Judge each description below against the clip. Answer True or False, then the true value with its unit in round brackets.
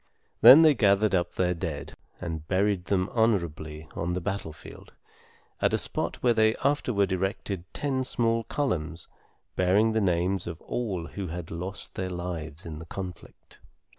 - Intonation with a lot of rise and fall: False (4.3 semitones)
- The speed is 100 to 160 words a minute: True (155 wpm)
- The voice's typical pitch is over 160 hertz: False (95 Hz)